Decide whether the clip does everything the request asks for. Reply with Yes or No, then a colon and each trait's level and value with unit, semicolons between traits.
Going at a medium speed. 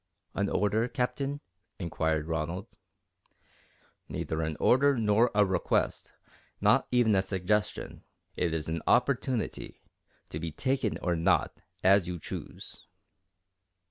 No: slow, 115 wpm